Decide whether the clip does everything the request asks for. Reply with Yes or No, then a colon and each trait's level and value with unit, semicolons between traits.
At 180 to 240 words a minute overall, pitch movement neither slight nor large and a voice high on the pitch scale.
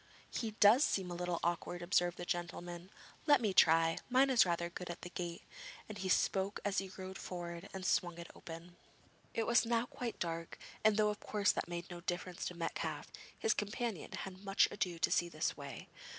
No: average, 200 wpm; average, 3.1 semitones; medium, 180 Hz